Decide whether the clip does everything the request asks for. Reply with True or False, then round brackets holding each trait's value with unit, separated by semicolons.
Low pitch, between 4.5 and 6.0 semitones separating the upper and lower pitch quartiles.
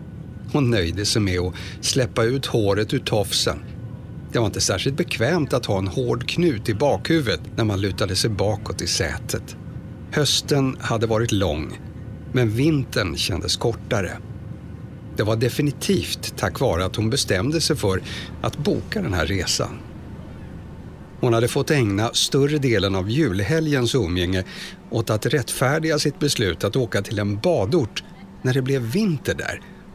True (115 Hz; 5.3 semitones)